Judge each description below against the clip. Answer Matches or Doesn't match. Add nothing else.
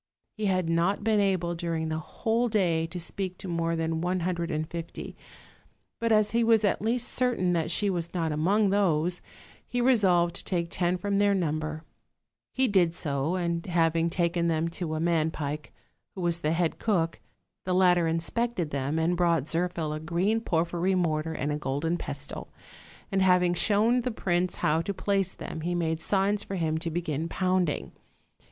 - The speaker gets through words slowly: Doesn't match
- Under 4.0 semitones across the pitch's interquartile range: Matches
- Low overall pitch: Doesn't match